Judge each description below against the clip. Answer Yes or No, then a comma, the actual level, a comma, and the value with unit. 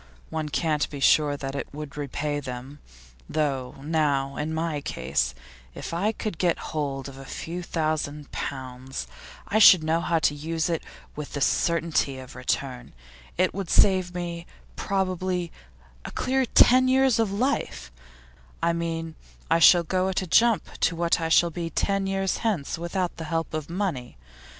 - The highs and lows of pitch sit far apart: No, average, 4.1 semitones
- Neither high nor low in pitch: Yes, medium, 165 Hz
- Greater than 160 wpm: Yes, average, 170 wpm